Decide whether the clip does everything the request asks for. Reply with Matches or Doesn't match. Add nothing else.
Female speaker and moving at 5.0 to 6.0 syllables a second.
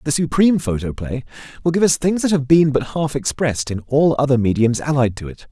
Doesn't match